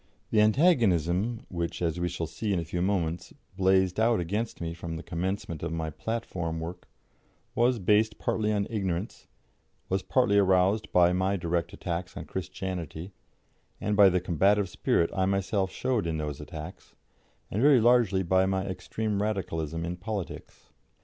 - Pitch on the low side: Yes, very low, 95 Hz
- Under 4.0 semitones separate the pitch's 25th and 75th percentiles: Yes, average, 3.5 semitones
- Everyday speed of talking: Yes, average, 160 wpm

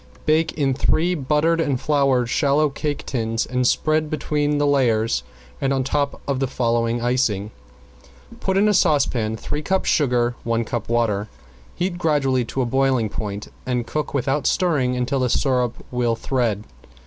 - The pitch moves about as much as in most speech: Yes, average, 3.9 semitones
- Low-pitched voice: Yes, low, 130 Hz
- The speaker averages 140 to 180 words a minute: Yes, average, 160 wpm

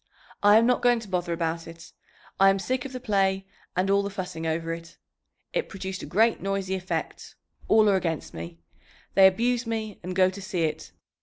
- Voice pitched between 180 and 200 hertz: Yes, high, 190 Hz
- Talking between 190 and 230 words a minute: Yes, fast, 205 wpm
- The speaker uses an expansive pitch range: No, average, 4.0 semitones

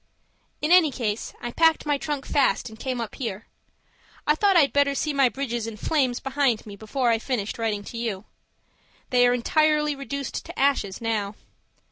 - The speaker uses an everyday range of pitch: Yes, average, 4.1 semitones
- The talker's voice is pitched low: No, very high, 255 Hz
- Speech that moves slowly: No, average, 180 wpm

